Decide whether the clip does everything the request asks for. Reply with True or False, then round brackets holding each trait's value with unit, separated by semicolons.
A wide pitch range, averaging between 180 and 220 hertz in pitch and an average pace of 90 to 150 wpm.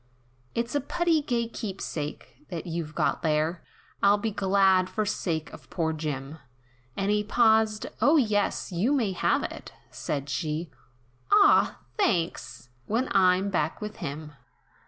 True (6.0 semitones; 190 Hz; 145 wpm)